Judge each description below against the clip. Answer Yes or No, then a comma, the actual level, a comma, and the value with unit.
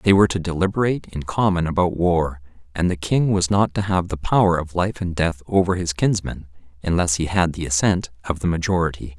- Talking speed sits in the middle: No, fast, 210 wpm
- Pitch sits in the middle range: No, very low, 85 Hz